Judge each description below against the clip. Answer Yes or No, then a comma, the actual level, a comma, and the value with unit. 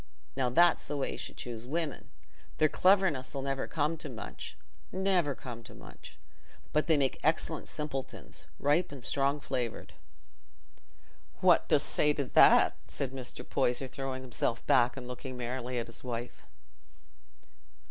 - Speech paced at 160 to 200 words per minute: No, average, 145 wpm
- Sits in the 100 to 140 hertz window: Yes, low, 135 Hz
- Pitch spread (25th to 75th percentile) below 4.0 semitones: Yes, average, 3.2 semitones